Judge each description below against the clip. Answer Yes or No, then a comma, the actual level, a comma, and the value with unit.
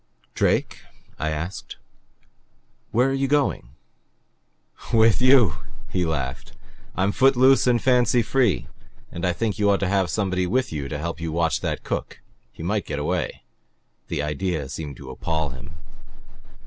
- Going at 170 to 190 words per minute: No, average, 150 wpm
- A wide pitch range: Yes, wide, 7.6 semitones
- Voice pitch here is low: Yes, very low, 90 Hz